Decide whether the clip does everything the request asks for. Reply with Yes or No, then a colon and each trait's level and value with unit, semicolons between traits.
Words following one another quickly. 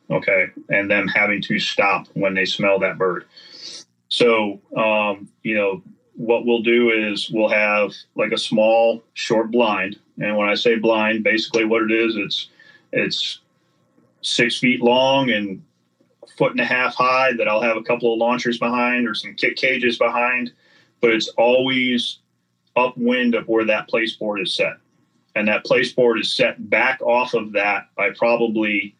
No: average, 170 wpm